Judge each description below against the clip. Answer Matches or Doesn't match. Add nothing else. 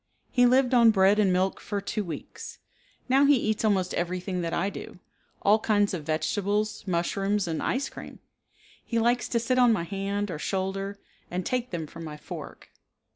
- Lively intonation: Doesn't match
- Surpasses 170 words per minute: Matches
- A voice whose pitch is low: Doesn't match